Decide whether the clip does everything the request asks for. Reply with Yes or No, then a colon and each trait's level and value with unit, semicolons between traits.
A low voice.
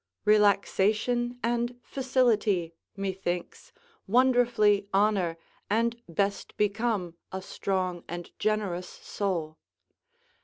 No: high, 205 Hz